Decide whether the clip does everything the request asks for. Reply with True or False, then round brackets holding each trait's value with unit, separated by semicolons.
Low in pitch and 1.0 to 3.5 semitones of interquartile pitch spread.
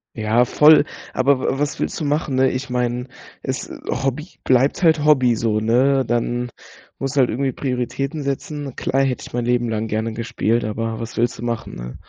True (125 Hz; 2.8 semitones)